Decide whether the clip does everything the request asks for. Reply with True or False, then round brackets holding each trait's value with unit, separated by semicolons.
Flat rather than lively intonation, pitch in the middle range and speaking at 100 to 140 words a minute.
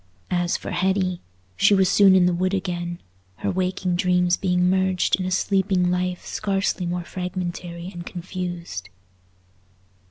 True (1.2 semitones; 180 Hz; 135 wpm)